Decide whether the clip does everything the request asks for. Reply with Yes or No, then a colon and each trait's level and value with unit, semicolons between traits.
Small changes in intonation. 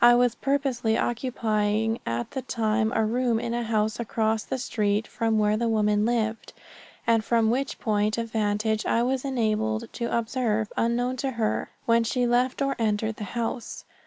Yes: narrow, 1.9 semitones